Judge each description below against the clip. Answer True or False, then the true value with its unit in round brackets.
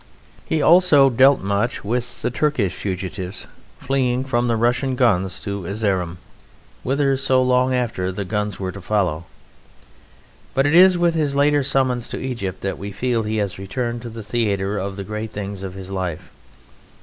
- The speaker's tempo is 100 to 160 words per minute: False (175 wpm)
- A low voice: True (115 Hz)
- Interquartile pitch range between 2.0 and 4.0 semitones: False (5.0 semitones)